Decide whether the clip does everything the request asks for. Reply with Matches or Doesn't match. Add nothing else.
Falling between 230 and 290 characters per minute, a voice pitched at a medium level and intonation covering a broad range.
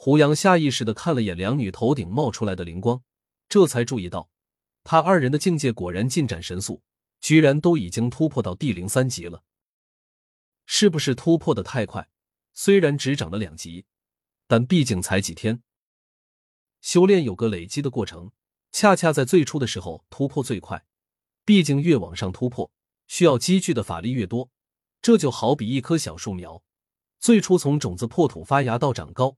Doesn't match